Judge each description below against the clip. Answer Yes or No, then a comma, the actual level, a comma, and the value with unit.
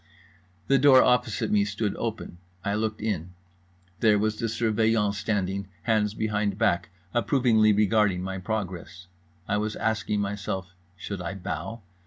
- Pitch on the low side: Yes, low, 105 Hz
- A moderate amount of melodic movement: No, narrow, 2.3 semitones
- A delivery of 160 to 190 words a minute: No, average, 140 wpm